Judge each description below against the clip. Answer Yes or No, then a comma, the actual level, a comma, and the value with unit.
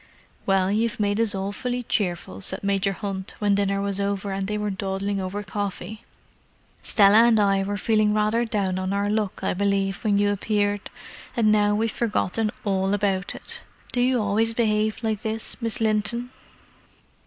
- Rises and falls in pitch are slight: Yes, narrow, 1.7 semitones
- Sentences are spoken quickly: No, average, 170 wpm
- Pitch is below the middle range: No, high, 205 Hz